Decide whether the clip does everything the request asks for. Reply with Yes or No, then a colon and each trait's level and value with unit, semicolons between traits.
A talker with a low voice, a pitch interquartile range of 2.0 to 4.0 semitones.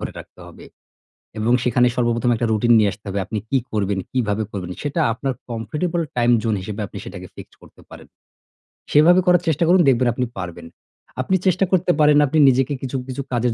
No: low, 125 Hz; wide, 5.4 semitones